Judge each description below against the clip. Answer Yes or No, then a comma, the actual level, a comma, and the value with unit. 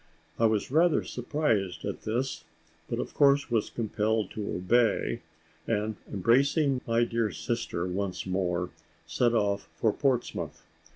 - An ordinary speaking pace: No, slow, 130 wpm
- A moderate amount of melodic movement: Yes, average, 3.7 semitones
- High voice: No, low, 115 Hz